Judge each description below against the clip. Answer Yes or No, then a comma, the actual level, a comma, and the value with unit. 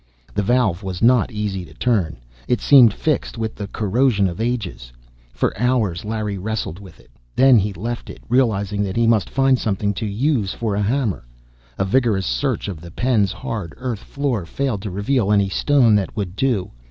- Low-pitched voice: Yes, low, 105 Hz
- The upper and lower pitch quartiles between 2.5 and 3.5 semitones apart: No, average, 4.1 semitones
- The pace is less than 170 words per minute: No, average, 190 wpm